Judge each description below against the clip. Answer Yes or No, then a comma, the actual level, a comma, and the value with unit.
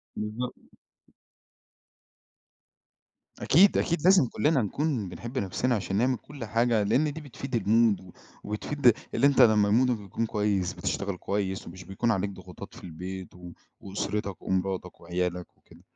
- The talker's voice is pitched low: Yes, low, 105 Hz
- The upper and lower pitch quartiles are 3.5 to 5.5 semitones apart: Yes, average, 4.7 semitones